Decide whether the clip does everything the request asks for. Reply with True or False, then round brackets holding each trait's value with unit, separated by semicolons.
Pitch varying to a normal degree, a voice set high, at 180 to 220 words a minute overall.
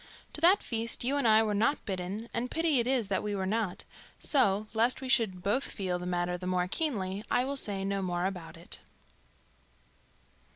True (4.9 semitones; 210 Hz; 200 wpm)